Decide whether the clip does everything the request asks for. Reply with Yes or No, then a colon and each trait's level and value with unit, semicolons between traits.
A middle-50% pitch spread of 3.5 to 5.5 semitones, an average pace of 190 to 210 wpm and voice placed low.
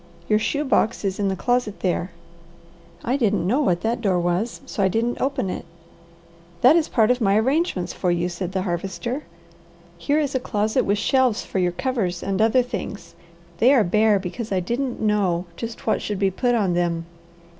No: average, 4.9 semitones; average, 200 wpm; high, 210 Hz